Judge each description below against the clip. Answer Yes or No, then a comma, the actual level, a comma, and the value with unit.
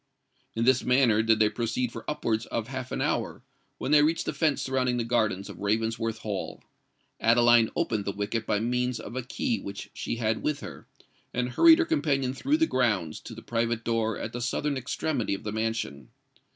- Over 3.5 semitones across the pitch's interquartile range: No, average, 2.9 semitones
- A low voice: Yes, low, 115 Hz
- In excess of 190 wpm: Yes, average, 200 wpm